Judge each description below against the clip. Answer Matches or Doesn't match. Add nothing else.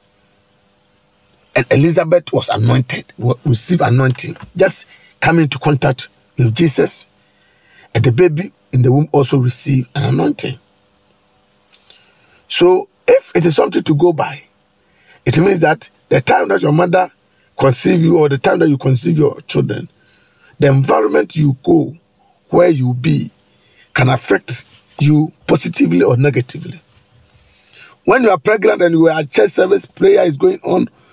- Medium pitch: Matches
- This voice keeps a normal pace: Matches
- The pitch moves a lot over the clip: Matches